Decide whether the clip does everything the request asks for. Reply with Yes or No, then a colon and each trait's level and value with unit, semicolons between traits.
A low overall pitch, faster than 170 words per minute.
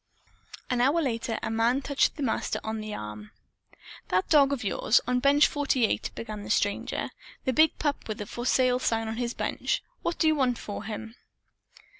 No: high, 240 Hz; average, 190 wpm